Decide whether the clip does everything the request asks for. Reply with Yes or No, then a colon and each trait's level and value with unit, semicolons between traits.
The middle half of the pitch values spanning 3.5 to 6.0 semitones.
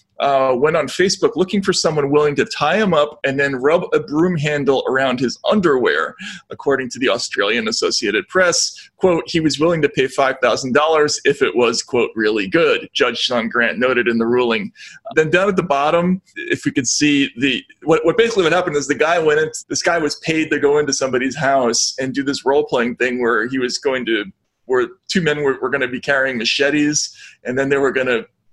Yes: average, 4.7 semitones